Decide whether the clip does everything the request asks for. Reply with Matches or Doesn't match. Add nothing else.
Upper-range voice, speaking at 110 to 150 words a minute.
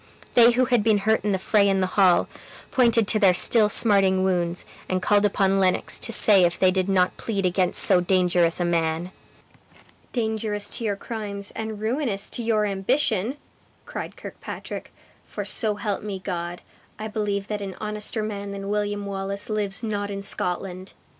Doesn't match